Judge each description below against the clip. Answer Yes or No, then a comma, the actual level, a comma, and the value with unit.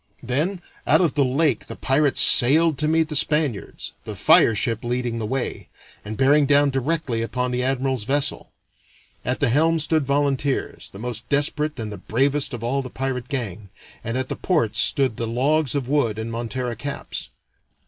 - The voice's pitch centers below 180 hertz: Yes, low, 135 Hz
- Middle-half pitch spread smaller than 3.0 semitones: No, average, 3.5 semitones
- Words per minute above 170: Yes, average, 180 wpm